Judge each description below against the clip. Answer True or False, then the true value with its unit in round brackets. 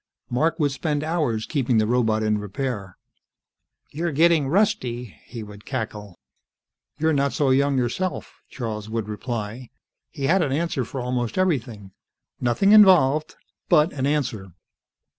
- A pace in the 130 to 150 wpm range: True (140 wpm)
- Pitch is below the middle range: True (130 Hz)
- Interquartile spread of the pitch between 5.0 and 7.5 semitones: True (5.6 semitones)